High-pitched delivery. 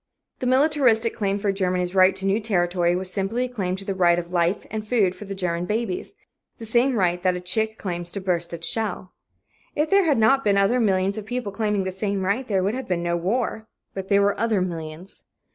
Yes: high, 195 Hz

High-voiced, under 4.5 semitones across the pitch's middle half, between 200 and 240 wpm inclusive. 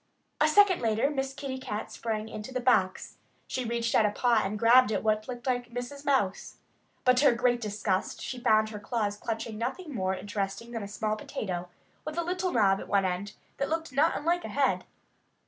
Yes: high, 230 Hz; average, 4.1 semitones; fast, 205 wpm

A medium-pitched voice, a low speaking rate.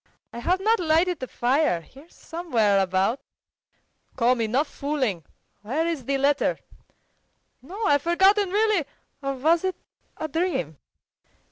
No: very high, 290 Hz; slow, 130 wpm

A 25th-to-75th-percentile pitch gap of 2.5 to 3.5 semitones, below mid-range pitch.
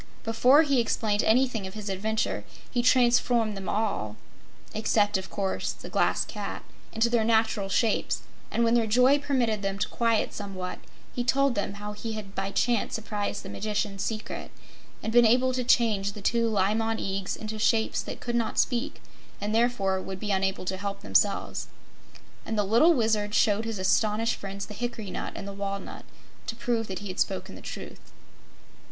No: average, 2.8 semitones; high, 220 Hz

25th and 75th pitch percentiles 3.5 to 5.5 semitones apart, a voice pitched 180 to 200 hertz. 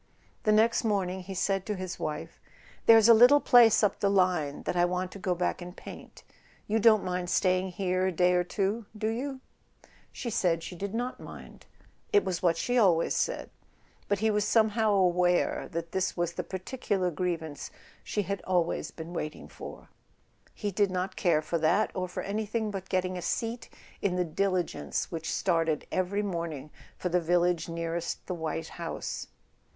No: average, 3.0 semitones; medium, 185 Hz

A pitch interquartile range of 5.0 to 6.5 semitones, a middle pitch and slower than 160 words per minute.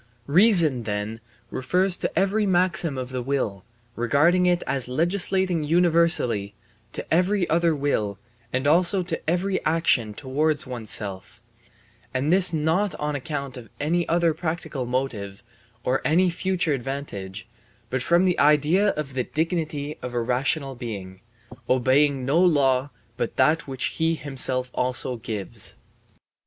Yes: average, 5.3 semitones; medium, 145 Hz; slow, 135 wpm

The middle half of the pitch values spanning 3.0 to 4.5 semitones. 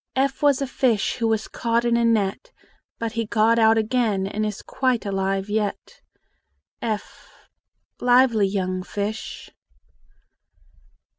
No: narrow, 2.5 semitones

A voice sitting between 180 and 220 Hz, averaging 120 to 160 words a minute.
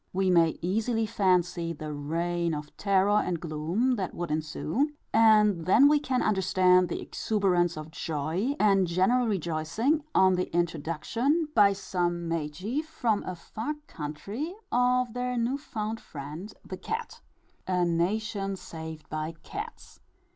Yes: medium, 185 Hz; average, 140 wpm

